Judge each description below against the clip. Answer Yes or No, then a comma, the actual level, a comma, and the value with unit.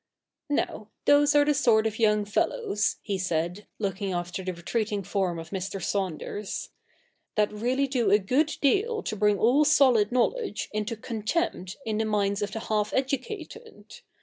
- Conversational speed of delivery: Yes, average, 170 wpm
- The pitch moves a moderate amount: Yes, average, 5.0 semitones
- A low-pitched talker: No, high, 215 Hz